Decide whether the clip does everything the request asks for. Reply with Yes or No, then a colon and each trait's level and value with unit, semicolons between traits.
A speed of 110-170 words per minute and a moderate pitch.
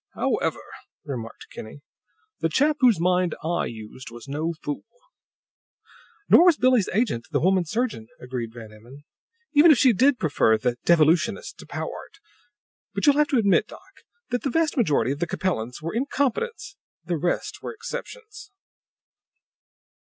Yes: average, 150 wpm; medium, 175 Hz